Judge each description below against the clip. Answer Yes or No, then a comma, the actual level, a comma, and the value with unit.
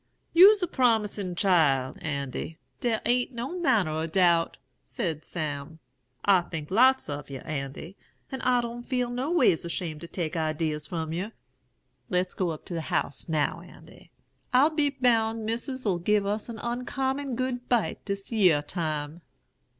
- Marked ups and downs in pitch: Yes, wide, 7.5 semitones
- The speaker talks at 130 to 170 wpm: Yes, average, 160 wpm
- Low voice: No, high, 195 Hz